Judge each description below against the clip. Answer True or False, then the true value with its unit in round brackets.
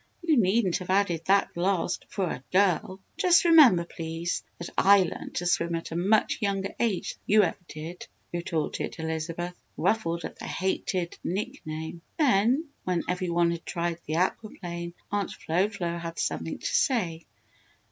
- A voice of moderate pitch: True (180 Hz)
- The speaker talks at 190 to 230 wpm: False (165 wpm)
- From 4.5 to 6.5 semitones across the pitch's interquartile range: False (3.0 semitones)